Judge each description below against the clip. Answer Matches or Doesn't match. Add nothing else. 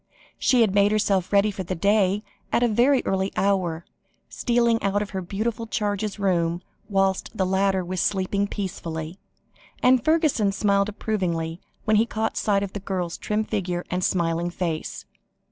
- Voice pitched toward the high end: Matches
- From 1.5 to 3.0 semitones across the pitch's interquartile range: Matches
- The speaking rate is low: Doesn't match